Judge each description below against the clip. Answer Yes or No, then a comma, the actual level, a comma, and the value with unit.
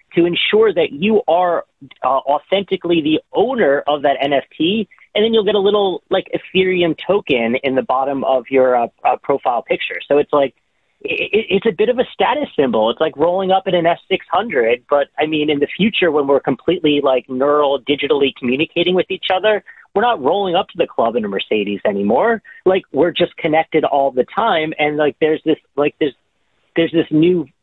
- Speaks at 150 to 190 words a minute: No, average, 200 wpm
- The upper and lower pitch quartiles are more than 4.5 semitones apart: Yes, average, 5.2 semitones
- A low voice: No, medium, 160 Hz